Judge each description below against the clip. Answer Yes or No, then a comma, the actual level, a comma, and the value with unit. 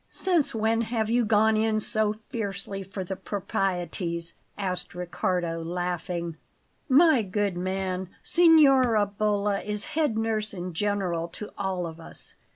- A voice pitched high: Yes, high, 200 Hz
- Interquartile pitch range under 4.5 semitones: Yes, average, 3.5 semitones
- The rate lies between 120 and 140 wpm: Yes, slow, 135 wpm